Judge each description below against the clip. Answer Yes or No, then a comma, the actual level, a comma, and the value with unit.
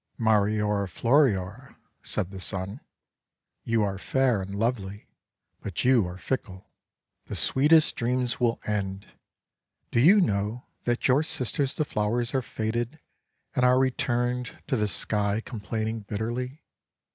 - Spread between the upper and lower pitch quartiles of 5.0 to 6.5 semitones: No, average, 3.8 semitones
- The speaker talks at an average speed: No, slow, 130 wpm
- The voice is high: No, low, 115 Hz